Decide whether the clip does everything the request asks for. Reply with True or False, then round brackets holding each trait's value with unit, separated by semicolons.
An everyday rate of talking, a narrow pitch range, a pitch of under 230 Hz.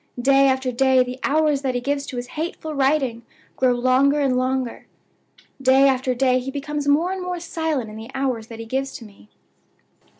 False (195 wpm; 2.2 semitones; 265 Hz)